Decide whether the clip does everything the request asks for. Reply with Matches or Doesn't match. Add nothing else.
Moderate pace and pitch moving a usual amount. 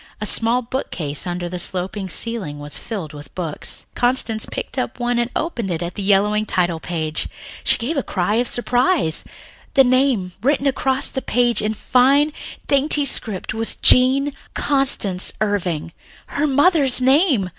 Doesn't match